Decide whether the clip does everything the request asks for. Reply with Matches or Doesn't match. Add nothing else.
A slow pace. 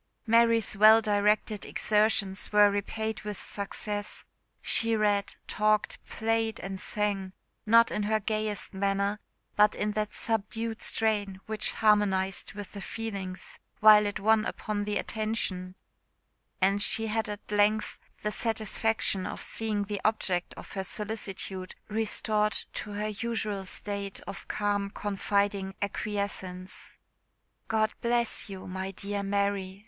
Matches